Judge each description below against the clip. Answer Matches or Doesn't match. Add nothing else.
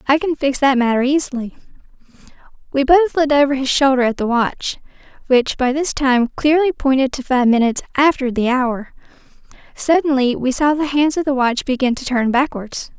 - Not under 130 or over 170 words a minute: Doesn't match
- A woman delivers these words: Matches